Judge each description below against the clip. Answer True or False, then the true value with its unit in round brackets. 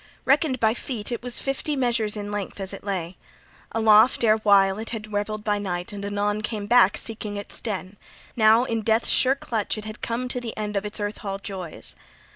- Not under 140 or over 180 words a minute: False (205 wpm)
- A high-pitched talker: True (215 Hz)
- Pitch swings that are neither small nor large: False (2.2 semitones)